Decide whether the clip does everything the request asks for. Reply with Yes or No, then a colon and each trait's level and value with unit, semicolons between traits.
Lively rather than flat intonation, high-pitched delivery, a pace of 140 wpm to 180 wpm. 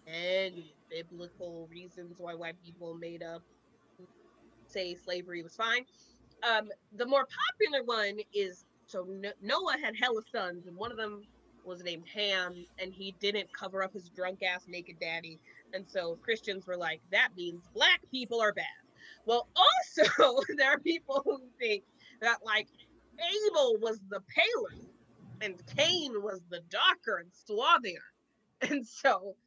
Yes: wide, 6.2 semitones; high, 205 Hz; average, 150 wpm